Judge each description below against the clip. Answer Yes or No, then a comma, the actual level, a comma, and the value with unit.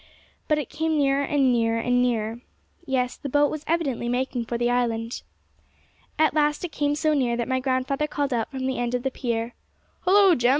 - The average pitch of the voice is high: Yes, very high, 260 Hz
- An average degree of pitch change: Yes, average, 3.4 semitones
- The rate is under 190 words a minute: No, fast, 205 wpm